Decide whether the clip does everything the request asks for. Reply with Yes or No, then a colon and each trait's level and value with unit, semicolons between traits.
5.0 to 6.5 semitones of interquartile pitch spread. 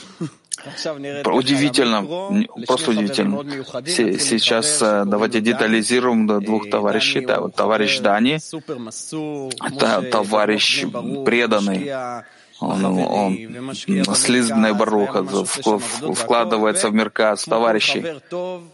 Yes: average, 5.3 semitones